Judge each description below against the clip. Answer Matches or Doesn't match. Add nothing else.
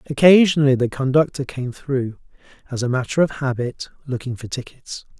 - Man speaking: Matches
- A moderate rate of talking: Matches